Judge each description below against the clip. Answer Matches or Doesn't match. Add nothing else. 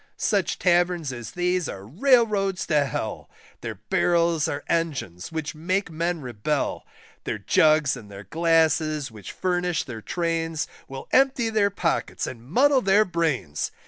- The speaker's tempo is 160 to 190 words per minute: Doesn't match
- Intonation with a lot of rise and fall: Doesn't match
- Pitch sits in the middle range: Matches